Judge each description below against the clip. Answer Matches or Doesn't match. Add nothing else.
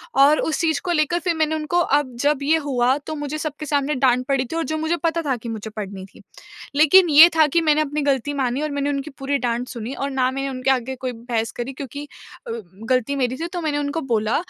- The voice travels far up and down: Doesn't match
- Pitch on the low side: Doesn't match